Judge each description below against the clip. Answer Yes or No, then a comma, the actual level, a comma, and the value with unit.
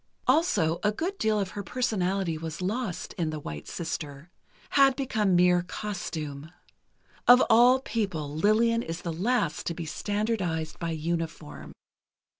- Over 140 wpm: No, slow, 135 wpm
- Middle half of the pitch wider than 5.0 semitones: Yes, wide, 5.4 semitones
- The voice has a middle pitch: Yes, medium, 180 Hz